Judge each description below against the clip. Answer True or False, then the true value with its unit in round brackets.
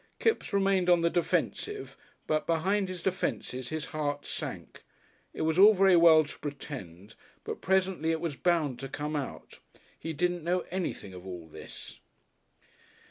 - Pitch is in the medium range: True (165 Hz)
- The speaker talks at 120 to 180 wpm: True (155 wpm)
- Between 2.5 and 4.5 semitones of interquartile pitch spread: True (4.2 semitones)